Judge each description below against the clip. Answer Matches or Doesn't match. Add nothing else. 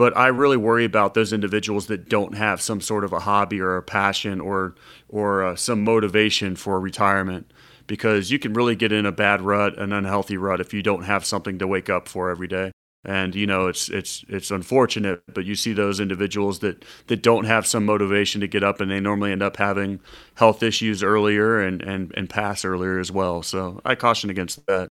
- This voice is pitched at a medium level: Doesn't match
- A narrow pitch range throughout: Matches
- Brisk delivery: Matches